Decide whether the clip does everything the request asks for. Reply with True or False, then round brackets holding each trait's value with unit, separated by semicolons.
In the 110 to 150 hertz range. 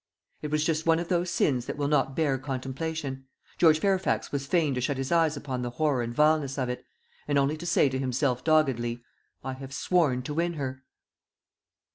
True (140 Hz)